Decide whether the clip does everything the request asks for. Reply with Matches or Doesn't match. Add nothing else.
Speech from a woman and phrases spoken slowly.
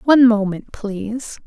Matches